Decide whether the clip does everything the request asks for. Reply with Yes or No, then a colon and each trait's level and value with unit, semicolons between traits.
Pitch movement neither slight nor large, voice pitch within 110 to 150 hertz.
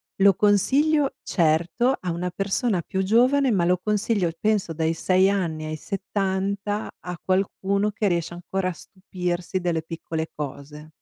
No: average, 3.2 semitones; high, 190 Hz